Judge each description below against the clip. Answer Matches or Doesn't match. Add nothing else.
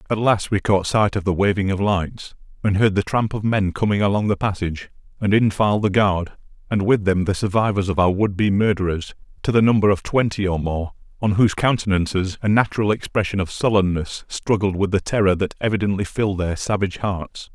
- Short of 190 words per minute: Doesn't match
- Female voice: Doesn't match